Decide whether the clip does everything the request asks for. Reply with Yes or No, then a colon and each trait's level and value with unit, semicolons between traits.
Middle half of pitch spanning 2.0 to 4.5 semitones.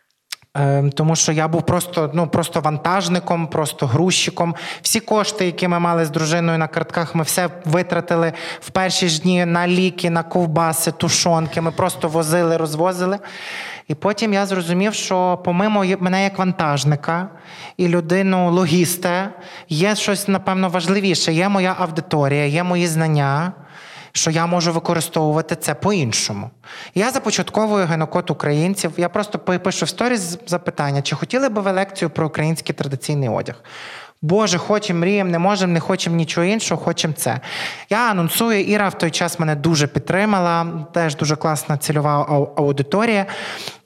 Yes: narrow, 2.6 semitones